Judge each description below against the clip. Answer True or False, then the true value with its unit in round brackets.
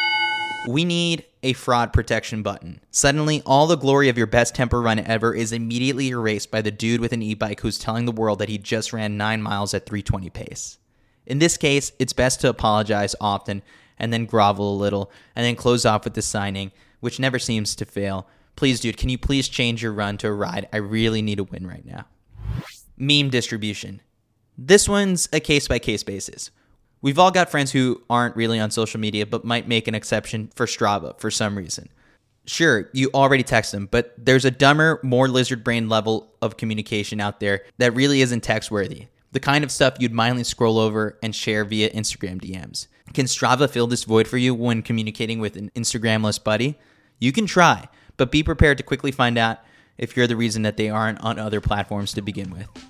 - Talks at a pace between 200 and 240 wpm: True (205 wpm)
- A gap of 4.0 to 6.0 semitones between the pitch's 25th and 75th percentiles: False (3.4 semitones)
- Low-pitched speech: True (115 Hz)